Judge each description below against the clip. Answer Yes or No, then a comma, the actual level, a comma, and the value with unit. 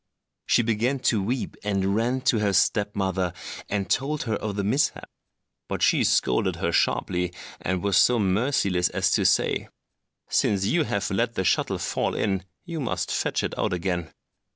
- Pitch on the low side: Yes, low, 100 Hz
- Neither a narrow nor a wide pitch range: Yes, average, 4.0 semitones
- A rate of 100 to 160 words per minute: No, average, 175 wpm